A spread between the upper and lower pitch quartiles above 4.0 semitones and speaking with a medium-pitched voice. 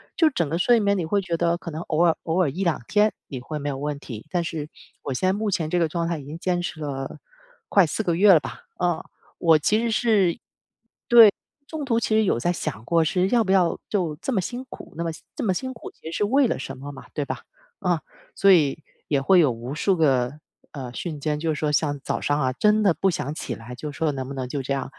Yes: average, 4.9 semitones; medium, 165 Hz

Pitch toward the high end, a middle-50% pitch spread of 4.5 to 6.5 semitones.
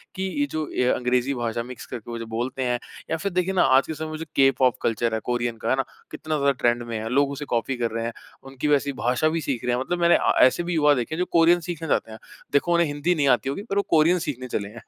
No: low, 135 Hz; average, 4.8 semitones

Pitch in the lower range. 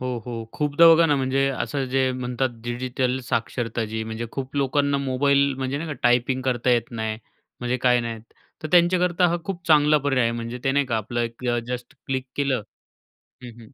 Yes: low, 130 Hz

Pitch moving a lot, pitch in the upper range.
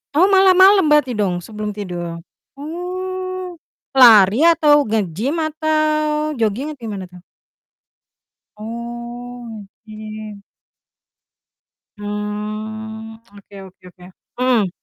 Yes: wide, 6.6 semitones; high, 230 Hz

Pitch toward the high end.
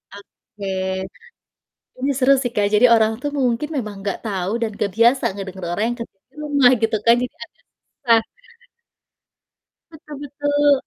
Yes: high, 235 Hz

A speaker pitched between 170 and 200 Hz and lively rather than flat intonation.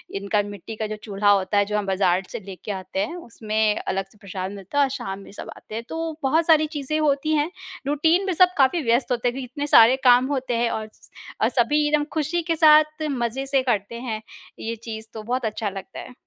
No: high, 235 Hz; wide, 5.7 semitones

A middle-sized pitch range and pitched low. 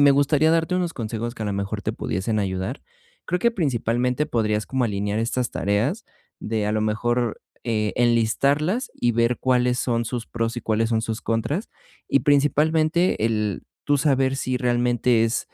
Yes: average, 4.0 semitones; low, 120 Hz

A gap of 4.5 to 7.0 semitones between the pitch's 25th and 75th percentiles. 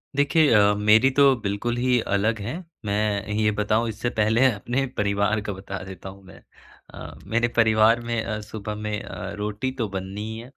No: narrow, 2.5 semitones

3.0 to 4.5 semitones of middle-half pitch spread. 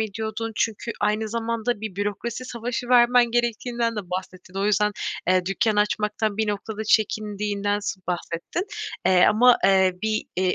No: narrow, 2.4 semitones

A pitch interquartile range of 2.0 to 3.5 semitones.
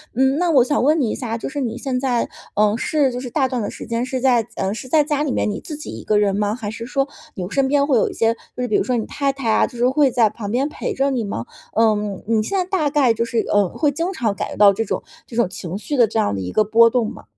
No: average, 4.3 semitones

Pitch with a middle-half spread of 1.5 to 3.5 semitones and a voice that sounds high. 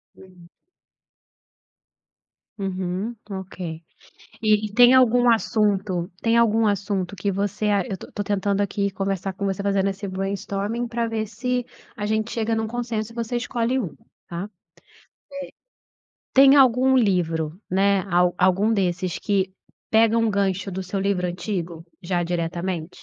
Yes: average, 3.2 semitones; high, 200 Hz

